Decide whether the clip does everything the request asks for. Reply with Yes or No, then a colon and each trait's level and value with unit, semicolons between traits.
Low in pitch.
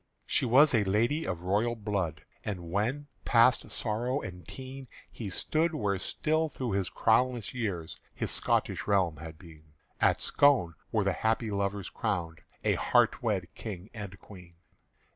Yes: low, 105 Hz